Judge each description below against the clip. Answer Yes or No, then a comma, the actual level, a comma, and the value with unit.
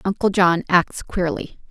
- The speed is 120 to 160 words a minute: Yes, average, 140 wpm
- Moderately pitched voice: Yes, medium, 180 Hz